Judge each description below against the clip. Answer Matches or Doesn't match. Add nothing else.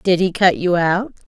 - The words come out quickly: Matches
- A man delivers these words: Doesn't match